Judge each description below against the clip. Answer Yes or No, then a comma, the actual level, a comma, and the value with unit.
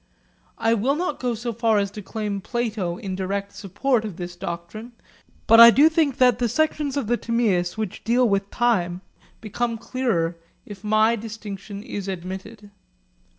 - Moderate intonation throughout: Yes, average, 3.4 semitones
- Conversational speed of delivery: Yes, average, 165 wpm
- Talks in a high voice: Yes, high, 220 Hz